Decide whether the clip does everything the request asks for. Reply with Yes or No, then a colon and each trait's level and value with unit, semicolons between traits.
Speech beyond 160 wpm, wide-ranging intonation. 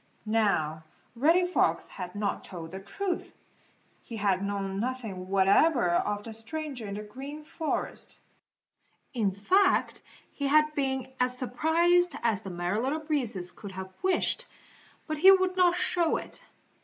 No: average, 145 wpm; wide, 7.8 semitones